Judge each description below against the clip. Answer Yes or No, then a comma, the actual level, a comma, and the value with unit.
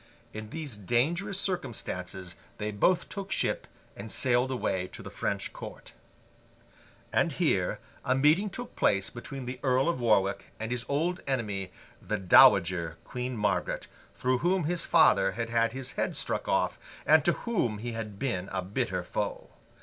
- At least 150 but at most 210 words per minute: Yes, average, 160 wpm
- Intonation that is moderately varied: No, wide, 5.7 semitones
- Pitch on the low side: Yes, low, 120 Hz